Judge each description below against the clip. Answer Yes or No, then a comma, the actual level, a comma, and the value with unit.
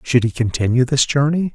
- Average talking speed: Yes, average, 195 wpm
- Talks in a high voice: No, low, 130 Hz